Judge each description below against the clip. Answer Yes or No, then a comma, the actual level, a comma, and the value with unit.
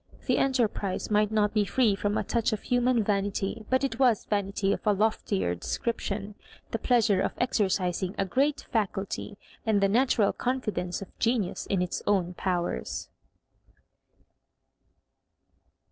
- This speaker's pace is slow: No, average, 145 wpm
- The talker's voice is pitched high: Yes, high, 210 Hz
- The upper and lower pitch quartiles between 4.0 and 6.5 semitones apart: No, average, 3.1 semitones